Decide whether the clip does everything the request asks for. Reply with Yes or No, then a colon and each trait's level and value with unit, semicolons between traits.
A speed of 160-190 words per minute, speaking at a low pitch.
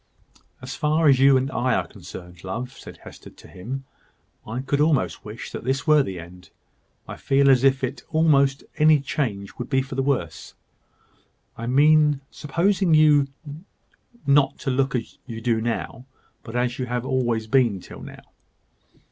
Yes: average, 165 wpm; low, 130 Hz